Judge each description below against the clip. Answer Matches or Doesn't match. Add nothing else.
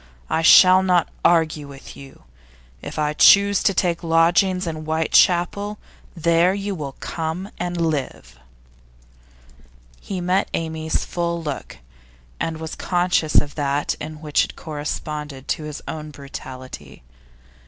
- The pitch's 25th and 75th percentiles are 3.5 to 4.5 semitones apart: Doesn't match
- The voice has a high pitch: Doesn't match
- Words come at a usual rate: Doesn't match